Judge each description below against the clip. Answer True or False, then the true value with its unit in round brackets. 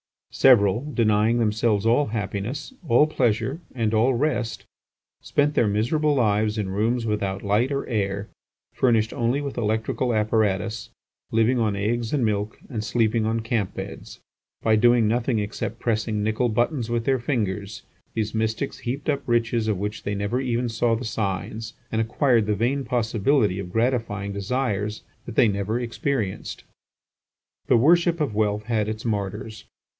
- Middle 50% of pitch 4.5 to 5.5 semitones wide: False (2.5 semitones)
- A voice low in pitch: True (115 Hz)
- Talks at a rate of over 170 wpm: False (155 wpm)